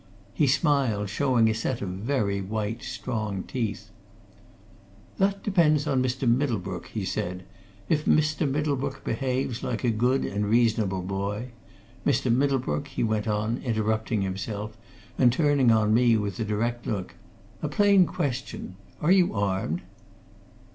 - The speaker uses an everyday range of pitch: Yes, average, 4.7 semitones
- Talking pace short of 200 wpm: Yes, average, 140 wpm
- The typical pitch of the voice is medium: No, low, 115 Hz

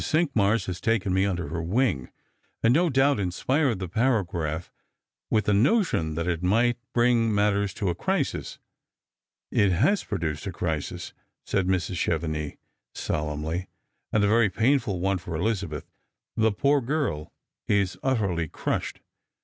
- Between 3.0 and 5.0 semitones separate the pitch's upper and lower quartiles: No, wide, 5.4 semitones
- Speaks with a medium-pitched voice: No, low, 100 Hz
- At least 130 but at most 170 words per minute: Yes, average, 150 wpm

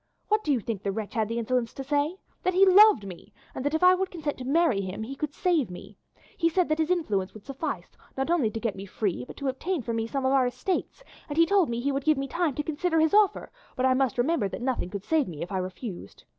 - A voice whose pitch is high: Yes, very high, 270 Hz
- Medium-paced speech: No, fast, 280 wpm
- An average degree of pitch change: No, wide, 6.6 semitones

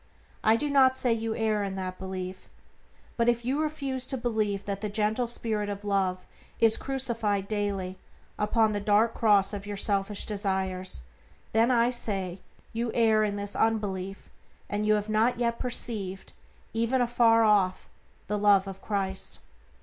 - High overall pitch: Yes, high, 210 Hz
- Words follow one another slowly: No, average, 155 wpm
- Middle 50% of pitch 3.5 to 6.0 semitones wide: No, average, 2.8 semitones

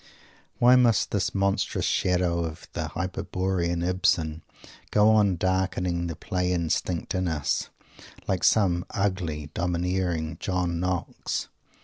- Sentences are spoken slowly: Yes, slow, 115 wpm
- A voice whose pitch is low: Yes, very low, 90 Hz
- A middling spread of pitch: No, narrow, 1.8 semitones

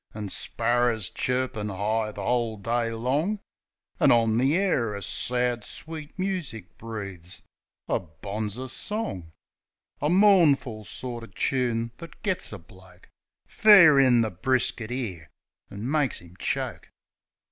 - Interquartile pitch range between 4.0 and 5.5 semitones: Yes, average, 4.4 semitones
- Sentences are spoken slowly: Yes, slow, 130 wpm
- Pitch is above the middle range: No, low, 120 Hz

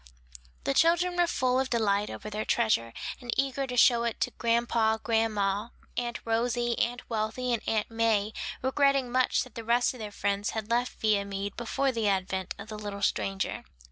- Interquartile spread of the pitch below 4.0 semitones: Yes, average, 2.9 semitones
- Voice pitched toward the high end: Yes, high, 230 Hz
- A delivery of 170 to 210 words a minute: Yes, average, 180 wpm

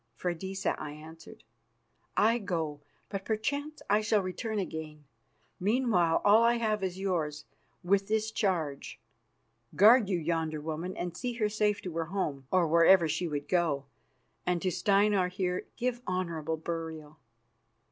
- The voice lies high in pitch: No, medium, 180 Hz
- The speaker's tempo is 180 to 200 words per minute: No, average, 145 wpm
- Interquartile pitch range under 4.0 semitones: No, average, 4.6 semitones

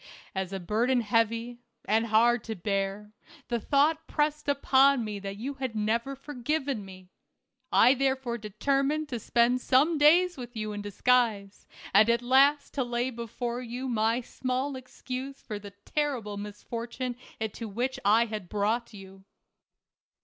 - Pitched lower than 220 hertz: No, high, 235 Hz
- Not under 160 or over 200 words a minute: No, average, 150 wpm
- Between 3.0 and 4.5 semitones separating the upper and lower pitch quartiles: Yes, average, 3.9 semitones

